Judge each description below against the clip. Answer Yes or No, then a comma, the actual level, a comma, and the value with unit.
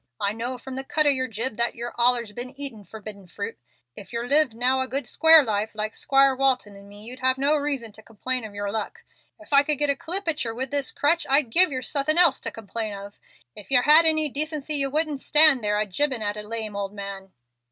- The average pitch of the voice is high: Yes, very high, 255 Hz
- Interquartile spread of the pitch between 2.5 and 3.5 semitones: No, average, 4.9 semitones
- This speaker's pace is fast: Yes, fast, 245 wpm